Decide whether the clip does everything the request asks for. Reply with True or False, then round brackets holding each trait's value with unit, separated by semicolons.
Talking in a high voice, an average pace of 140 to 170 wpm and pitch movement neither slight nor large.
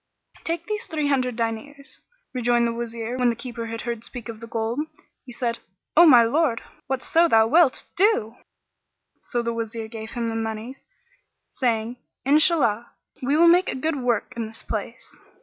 True (240 Hz; 165 wpm; 3.7 semitones)